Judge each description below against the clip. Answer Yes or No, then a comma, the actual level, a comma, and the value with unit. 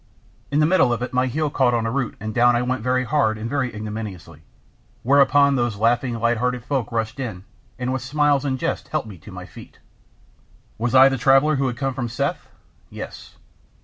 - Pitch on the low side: Yes, low, 125 Hz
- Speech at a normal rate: No, fast, 210 wpm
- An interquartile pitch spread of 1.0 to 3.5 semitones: Yes, average, 2.9 semitones